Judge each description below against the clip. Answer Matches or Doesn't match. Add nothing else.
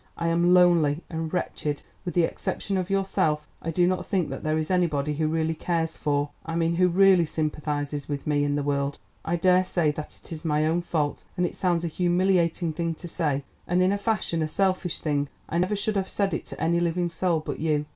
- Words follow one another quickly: Matches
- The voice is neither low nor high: Matches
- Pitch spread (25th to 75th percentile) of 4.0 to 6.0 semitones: Doesn't match